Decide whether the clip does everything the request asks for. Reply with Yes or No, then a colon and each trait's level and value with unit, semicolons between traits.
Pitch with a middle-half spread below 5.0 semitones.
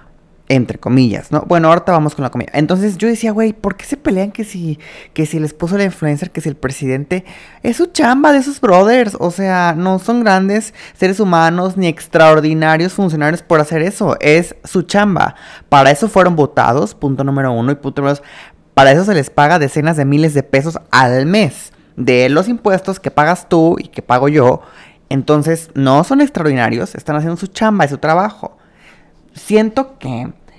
No: average, 5.3 semitones